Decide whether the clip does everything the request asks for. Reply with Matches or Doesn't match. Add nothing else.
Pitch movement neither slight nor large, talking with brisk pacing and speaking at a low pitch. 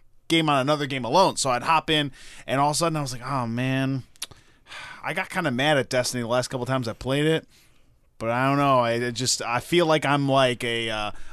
Matches